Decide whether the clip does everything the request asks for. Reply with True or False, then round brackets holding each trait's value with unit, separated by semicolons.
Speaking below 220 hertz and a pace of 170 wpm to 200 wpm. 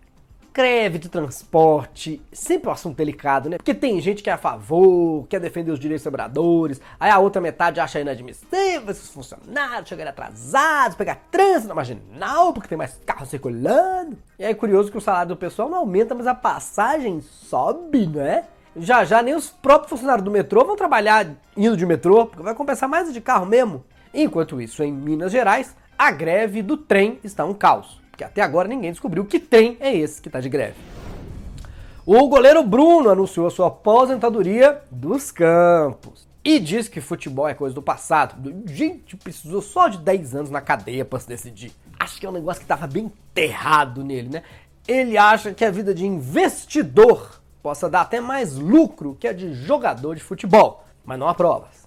True (190 Hz; 185 wpm)